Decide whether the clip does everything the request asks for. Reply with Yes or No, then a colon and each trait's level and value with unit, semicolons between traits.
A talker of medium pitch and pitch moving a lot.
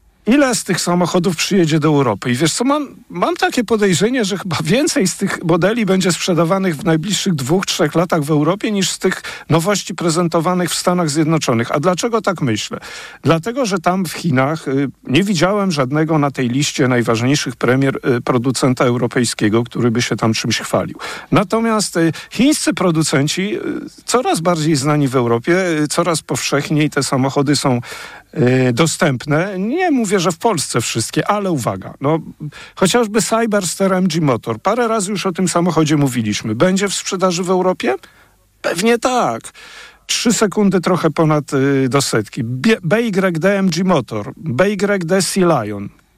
Yes: medium, 170 Hz; wide, 5.8 semitones